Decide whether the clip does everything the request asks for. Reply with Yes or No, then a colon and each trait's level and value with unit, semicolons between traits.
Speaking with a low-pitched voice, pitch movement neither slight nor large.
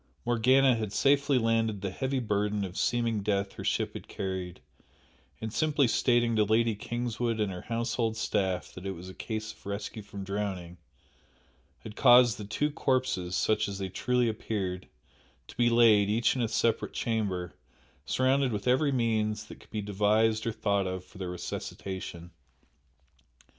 Yes: low, 110 Hz; average, 3.2 semitones